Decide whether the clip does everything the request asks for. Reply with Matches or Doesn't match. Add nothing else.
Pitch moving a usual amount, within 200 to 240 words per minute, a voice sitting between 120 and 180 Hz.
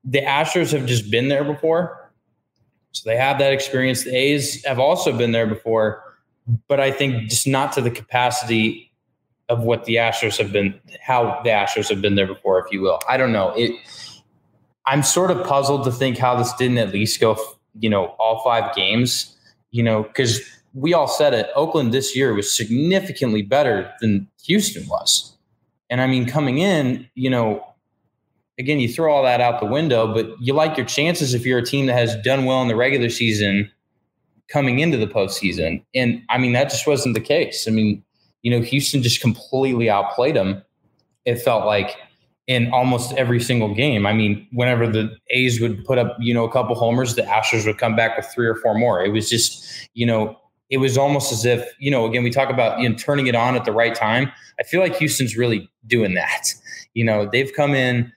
Matches